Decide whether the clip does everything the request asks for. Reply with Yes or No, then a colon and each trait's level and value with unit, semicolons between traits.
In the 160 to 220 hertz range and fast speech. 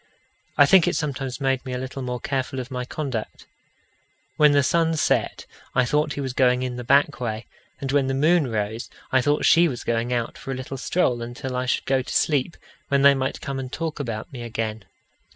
No: low, 130 Hz; fast, 220 wpm